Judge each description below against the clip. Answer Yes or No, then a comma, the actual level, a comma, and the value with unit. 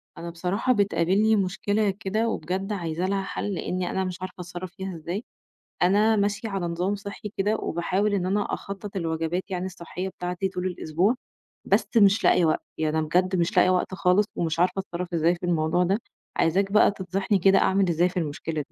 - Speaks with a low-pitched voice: No, medium, 185 Hz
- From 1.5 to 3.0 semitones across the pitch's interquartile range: Yes, narrow, 2.5 semitones